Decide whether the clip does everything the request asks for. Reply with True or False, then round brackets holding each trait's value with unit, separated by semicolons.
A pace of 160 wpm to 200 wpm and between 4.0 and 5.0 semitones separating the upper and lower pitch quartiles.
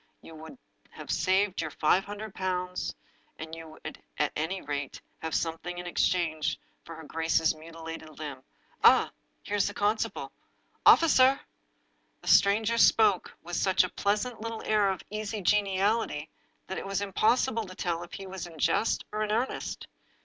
True (165 wpm; 4.4 semitones)